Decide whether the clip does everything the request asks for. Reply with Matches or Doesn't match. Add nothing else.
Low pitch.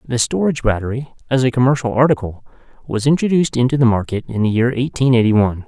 Matches